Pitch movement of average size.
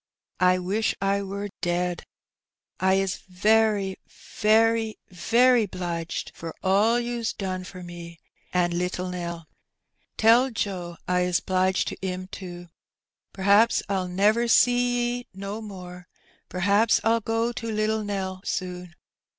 Yes: average, 3.6 semitones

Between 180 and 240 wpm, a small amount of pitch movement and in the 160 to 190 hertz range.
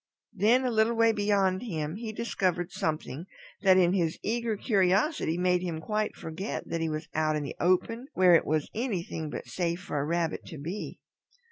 No: average, 190 wpm; average, 4.7 semitones; medium, 185 Hz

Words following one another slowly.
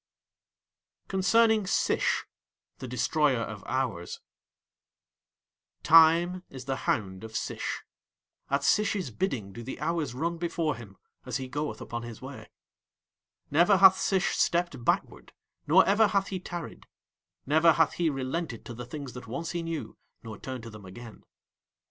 No: average, 145 wpm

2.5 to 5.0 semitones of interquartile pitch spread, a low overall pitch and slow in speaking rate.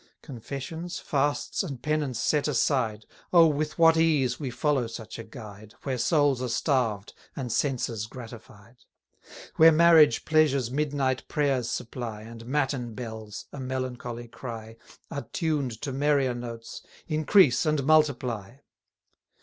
Yes: average, 4.2 semitones; low, 130 Hz; slow, 130 wpm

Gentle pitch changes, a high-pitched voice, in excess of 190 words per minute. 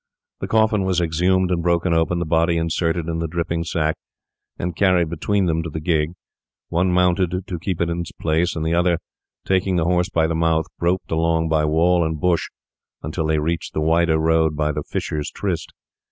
No: narrow, 1.8 semitones; very low, 85 Hz; average, 200 wpm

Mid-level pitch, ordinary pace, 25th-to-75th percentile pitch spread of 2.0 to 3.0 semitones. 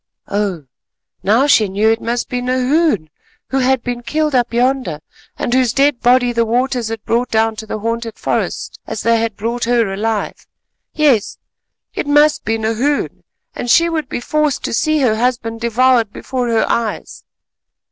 No: high, 240 Hz; average, 170 wpm; narrow, 2.6 semitones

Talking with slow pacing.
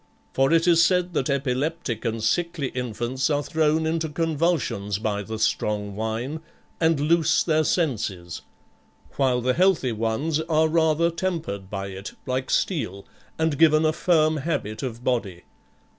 No: average, 145 wpm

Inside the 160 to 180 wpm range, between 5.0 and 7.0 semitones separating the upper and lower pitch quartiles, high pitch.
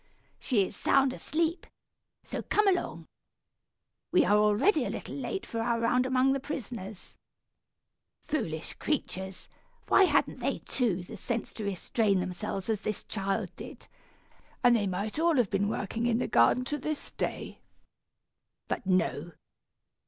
No: average, 145 wpm; wide, 5.5 semitones; high, 225 Hz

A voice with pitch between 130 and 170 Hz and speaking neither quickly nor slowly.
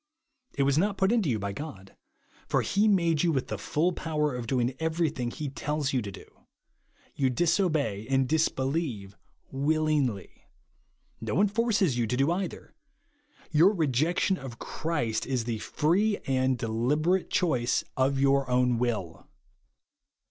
Yes: medium, 140 Hz; average, 150 wpm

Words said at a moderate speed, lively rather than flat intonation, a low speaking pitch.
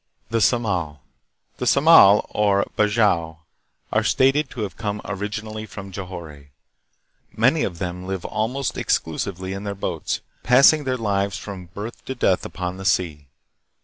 No: average, 145 wpm; average, 3.5 semitones; low, 100 Hz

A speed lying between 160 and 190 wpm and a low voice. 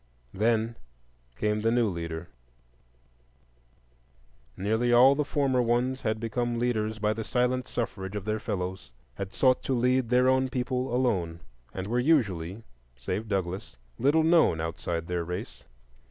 No: average, 140 wpm; low, 115 Hz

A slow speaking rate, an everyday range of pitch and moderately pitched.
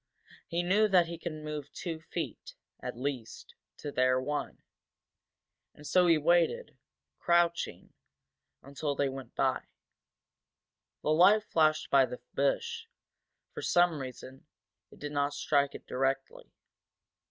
Yes: slow, 130 wpm; average, 3.8 semitones; medium, 150 Hz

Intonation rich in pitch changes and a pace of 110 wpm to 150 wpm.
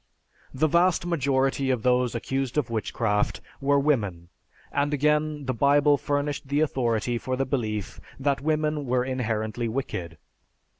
No: average, 3.6 semitones; average, 140 wpm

